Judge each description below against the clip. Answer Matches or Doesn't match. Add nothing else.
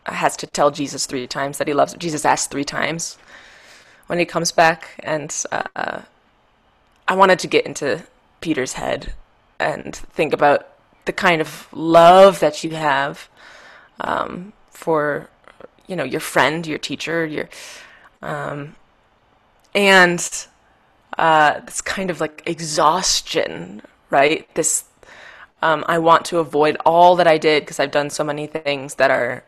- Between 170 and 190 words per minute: Doesn't match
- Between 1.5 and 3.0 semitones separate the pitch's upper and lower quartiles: Matches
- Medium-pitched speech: Matches